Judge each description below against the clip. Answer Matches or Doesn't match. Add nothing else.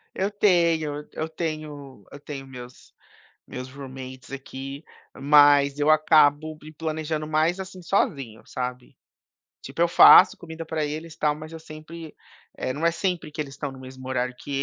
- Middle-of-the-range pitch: Matches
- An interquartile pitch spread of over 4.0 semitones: Doesn't match